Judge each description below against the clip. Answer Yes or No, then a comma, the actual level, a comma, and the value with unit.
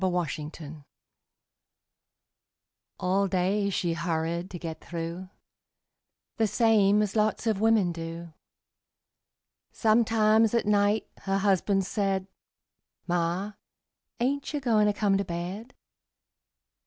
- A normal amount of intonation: Yes, average, 3.7 semitones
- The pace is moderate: No, slow, 110 wpm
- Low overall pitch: No, high, 195 Hz